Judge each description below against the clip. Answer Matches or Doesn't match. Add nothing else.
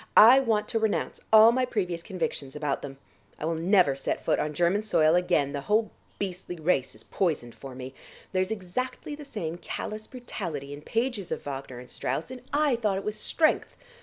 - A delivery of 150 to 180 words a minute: Doesn't match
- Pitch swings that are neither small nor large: Doesn't match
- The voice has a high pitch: Doesn't match